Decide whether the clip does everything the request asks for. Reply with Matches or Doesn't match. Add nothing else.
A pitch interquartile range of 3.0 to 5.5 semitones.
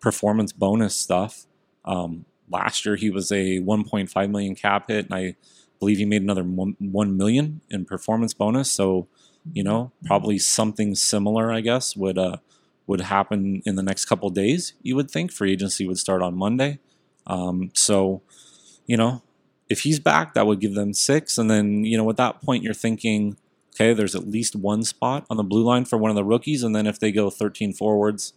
Doesn't match